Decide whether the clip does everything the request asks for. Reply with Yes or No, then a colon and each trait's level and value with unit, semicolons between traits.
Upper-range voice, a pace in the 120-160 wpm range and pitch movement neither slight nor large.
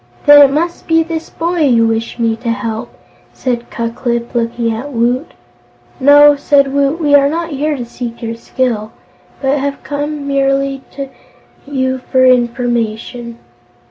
Yes: very high, 260 Hz; average, 155 wpm; average, 3.3 semitones